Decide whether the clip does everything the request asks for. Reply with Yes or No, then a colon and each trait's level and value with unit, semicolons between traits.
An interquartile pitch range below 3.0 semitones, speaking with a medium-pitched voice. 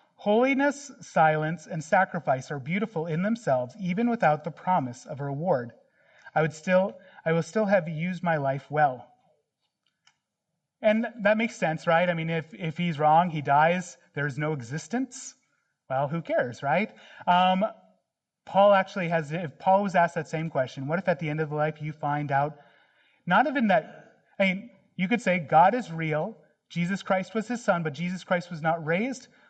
No: average, 4.1 semitones; medium, 170 Hz